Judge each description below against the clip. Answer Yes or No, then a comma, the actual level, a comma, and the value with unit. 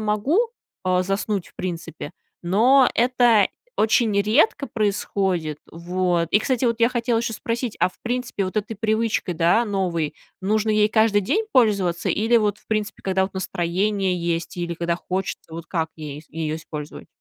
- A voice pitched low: No, high, 200 Hz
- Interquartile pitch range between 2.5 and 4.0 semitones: No, average, 4.4 semitones